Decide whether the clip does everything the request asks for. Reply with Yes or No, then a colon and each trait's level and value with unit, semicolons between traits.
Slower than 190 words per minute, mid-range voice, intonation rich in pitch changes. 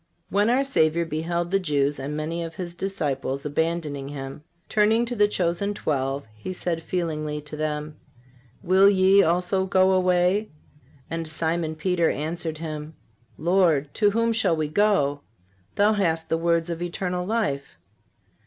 No: average, 150 wpm; medium, 170 Hz; average, 3.7 semitones